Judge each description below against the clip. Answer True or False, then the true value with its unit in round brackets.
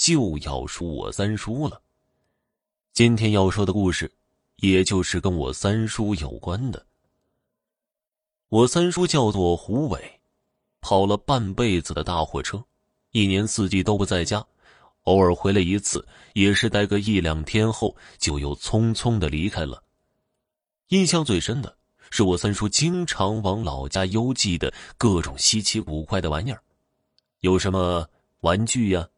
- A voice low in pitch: True (100 Hz)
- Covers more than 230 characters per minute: False (215 characters per minute)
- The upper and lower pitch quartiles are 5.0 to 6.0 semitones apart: False (4.3 semitones)